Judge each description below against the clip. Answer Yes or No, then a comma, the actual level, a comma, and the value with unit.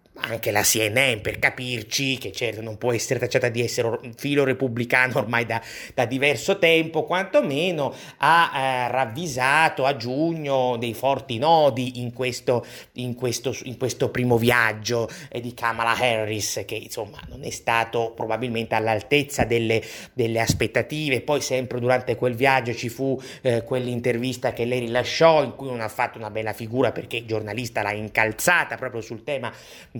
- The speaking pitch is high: No, low, 125 Hz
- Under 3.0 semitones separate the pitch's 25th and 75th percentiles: Yes, narrow, 2.4 semitones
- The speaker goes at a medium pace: Yes, average, 160 wpm